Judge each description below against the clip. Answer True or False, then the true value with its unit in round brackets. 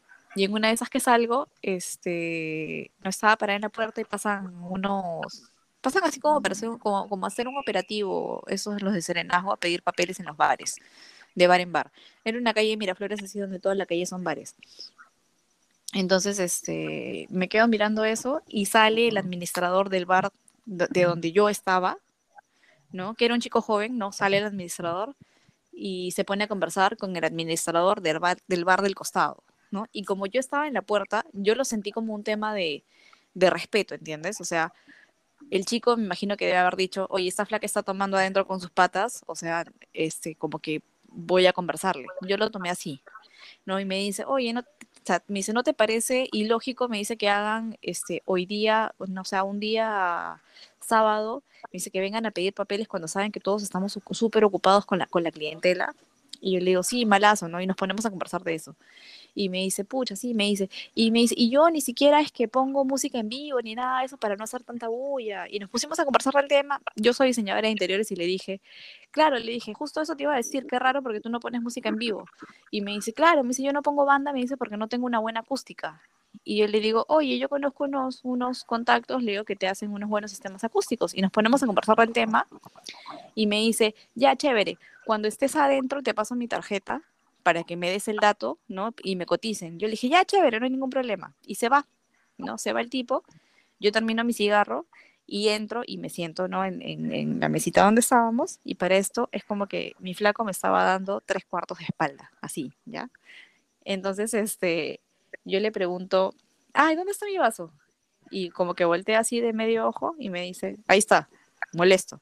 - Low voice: False (210 Hz)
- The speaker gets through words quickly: True (215 wpm)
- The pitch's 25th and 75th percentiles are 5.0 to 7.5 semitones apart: False (4.2 semitones)